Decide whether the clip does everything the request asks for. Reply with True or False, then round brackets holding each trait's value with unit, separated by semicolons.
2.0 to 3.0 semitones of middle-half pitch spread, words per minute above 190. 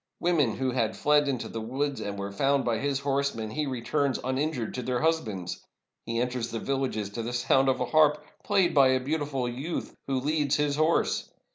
False (3.5 semitones; 200 wpm)